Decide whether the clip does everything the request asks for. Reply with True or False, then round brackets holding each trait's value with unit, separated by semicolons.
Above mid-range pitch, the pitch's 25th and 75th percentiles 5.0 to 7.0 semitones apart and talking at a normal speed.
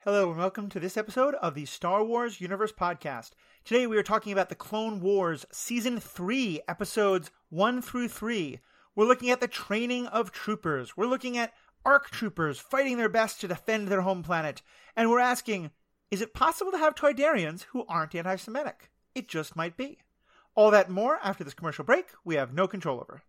True (210 Hz; 5.3 semitones; 195 wpm)